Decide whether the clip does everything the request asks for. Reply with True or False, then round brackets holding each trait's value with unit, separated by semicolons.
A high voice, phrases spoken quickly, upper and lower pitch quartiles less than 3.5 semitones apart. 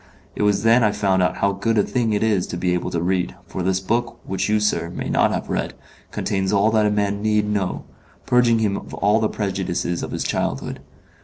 False (100 Hz; 230 wpm; 2.4 semitones)